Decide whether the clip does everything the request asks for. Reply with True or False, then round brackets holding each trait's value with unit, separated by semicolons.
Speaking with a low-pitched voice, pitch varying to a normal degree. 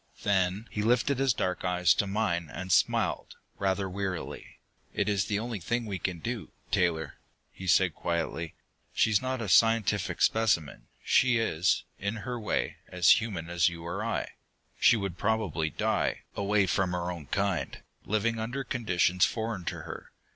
True (100 Hz; 4.0 semitones)